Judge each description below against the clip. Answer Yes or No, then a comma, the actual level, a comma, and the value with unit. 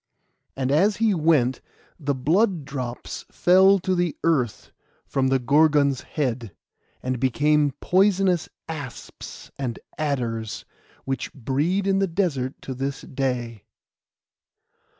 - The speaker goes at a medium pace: No, slow, 115 wpm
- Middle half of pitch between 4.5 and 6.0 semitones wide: Yes, average, 5.3 semitones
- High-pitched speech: No, medium, 145 Hz